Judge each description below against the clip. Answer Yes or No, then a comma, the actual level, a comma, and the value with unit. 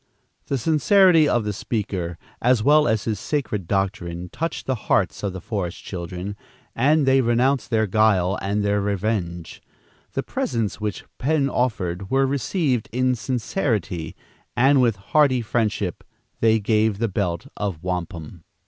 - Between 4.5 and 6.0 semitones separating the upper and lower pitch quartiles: Yes, average, 5.2 semitones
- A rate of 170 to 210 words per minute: No, average, 145 wpm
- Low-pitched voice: Yes, low, 110 Hz